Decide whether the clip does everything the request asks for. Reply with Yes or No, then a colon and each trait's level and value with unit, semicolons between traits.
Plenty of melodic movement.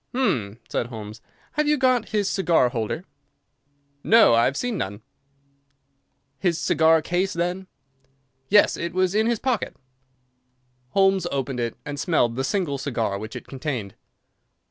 Yes: wide, 8.4 semitones